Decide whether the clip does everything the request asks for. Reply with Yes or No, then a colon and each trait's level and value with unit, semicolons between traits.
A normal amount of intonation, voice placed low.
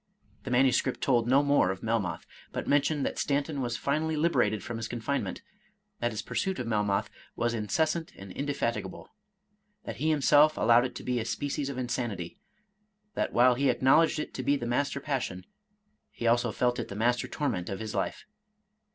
Yes: average, 4.1 semitones; low, 130 Hz